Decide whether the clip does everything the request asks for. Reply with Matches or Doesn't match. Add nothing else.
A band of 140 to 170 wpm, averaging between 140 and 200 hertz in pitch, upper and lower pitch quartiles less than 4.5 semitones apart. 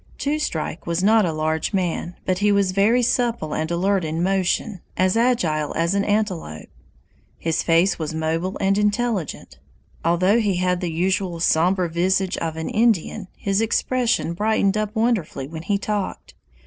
Matches